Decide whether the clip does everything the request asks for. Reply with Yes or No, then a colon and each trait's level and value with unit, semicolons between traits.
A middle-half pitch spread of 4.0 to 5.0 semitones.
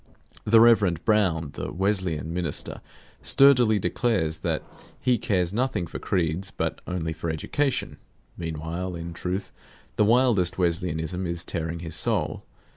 Yes: average, 4.3 semitones